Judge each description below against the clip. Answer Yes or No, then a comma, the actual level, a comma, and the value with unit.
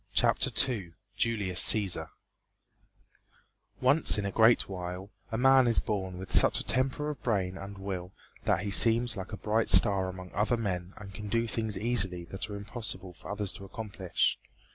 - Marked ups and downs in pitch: No, average, 3.4 semitones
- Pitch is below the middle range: Yes, low, 100 Hz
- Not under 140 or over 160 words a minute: No, average, 175 wpm